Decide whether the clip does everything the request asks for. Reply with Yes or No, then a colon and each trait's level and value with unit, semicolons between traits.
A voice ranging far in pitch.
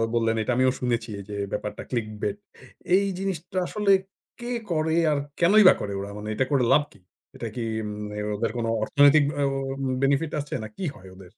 Yes: wide, 7.1 semitones